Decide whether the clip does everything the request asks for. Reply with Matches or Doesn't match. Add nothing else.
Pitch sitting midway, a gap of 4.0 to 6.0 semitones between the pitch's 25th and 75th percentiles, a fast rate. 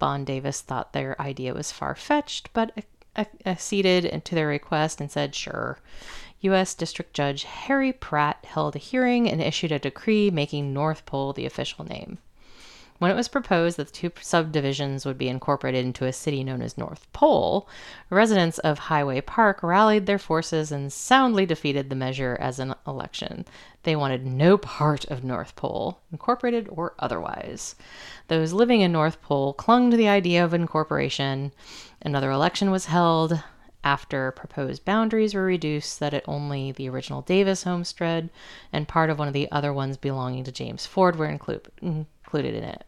Doesn't match